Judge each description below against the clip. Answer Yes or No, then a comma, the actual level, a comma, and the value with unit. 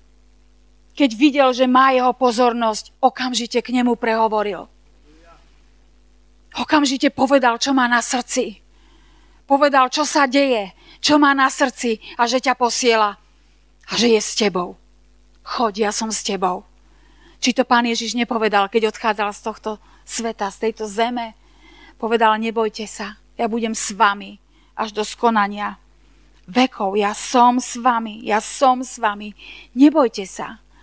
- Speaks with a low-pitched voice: No, high, 235 Hz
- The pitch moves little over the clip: No, average, 3.4 semitones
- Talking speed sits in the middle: Yes, average, 140 wpm